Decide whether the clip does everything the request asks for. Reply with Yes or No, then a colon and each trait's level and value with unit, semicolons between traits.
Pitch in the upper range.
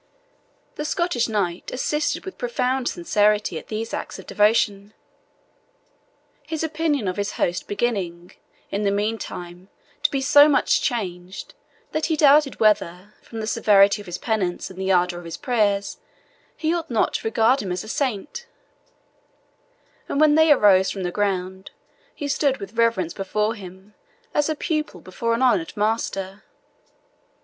Yes: high, 210 Hz